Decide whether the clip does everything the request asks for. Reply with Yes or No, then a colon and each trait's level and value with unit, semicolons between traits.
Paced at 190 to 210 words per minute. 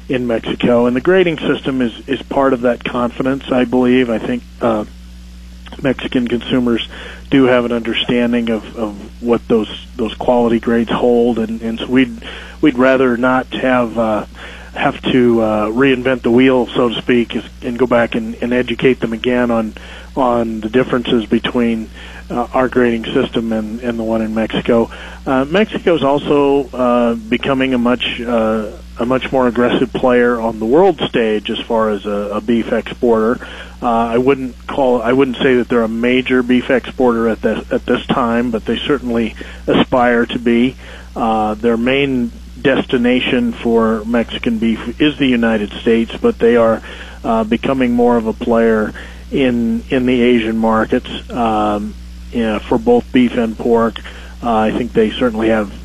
No: average, 170 wpm